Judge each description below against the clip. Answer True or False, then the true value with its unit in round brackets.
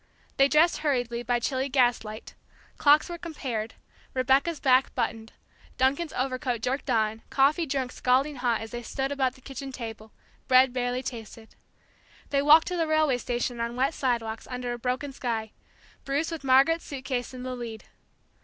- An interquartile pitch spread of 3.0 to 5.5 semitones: False (2.6 semitones)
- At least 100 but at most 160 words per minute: False (170 wpm)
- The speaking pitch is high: True (255 Hz)